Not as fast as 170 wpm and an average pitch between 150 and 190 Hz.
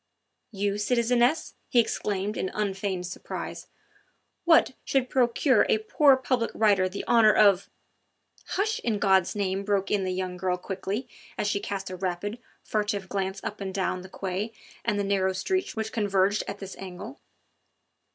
No: average, 160 wpm; high, 200 Hz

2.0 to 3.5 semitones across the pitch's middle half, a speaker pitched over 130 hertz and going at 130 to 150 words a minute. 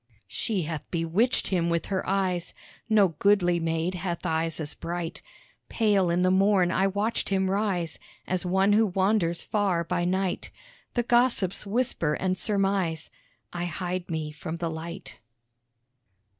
Yes: average, 2.7 semitones; medium, 185 Hz; average, 145 wpm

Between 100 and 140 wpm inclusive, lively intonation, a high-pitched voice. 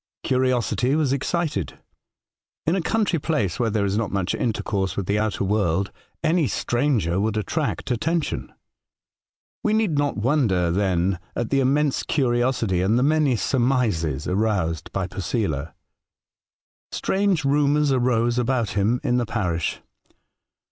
No: slow, 135 wpm; wide, 6.3 semitones; low, 120 Hz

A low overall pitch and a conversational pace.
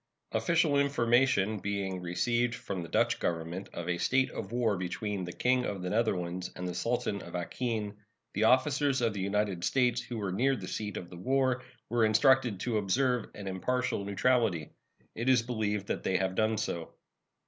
Yes: low, 110 Hz; average, 180 wpm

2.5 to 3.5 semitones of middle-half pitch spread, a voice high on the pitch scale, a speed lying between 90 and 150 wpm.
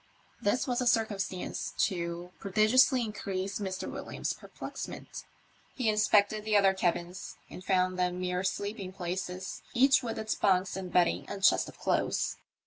Yes: average, 2.9 semitones; high, 195 Hz; average, 145 wpm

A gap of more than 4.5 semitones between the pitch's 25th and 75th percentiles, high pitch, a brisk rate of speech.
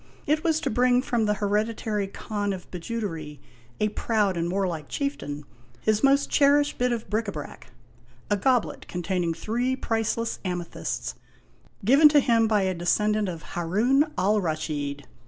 No: wide, 5.4 semitones; high, 210 Hz; average, 155 wpm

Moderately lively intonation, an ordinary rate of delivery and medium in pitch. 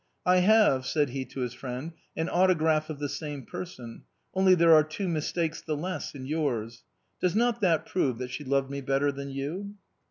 No: average, 4.7 semitones; fast, 215 wpm; medium, 150 Hz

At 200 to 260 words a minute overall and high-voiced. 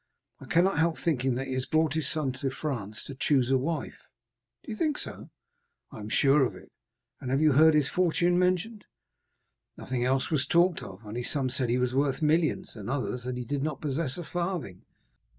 No: fast, 205 wpm; medium, 140 Hz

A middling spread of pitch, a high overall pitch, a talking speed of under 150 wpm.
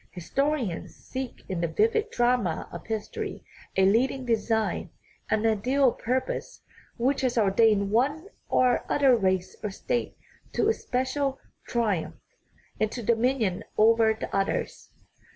Yes: average, 4.1 semitones; high, 230 Hz; slow, 135 wpm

